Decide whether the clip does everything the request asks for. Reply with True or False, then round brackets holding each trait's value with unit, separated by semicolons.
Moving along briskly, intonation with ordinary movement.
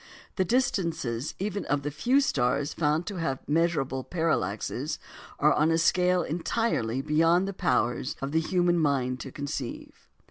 False (150 wpm; 4.6 semitones)